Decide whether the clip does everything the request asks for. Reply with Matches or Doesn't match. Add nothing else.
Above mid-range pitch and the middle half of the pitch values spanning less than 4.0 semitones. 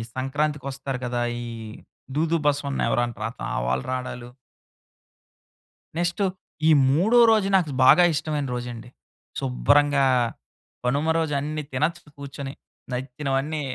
Doesn't match